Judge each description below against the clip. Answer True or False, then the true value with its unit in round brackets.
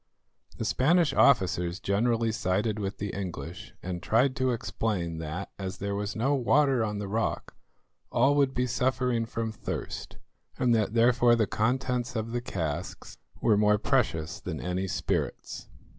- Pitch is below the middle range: True (110 Hz)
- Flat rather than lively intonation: False (4.2 semitones)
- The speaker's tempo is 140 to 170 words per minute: True (155 wpm)